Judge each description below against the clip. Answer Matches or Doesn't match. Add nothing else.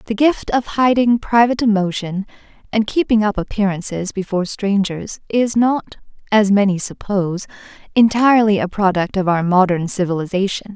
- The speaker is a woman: Matches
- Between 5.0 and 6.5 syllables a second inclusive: Matches